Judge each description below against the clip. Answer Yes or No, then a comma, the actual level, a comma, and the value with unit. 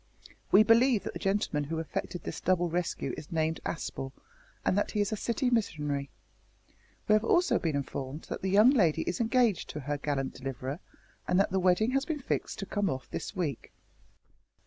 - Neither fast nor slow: Yes, average, 190 wpm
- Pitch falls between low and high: Yes, medium, 180 Hz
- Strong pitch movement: Yes, wide, 6.5 semitones